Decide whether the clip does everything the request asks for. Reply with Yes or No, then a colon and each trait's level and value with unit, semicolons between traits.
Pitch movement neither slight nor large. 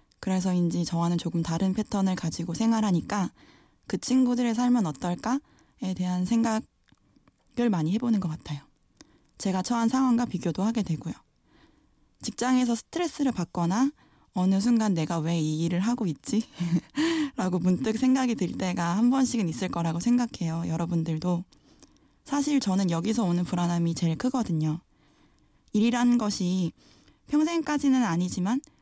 No: wide, 5.8 semitones